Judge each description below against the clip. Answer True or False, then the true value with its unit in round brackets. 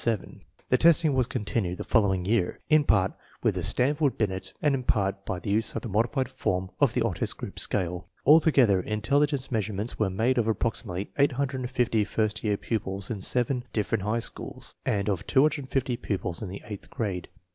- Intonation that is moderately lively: True (4.7 semitones)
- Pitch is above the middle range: False (110 Hz)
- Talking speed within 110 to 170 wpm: False (185 wpm)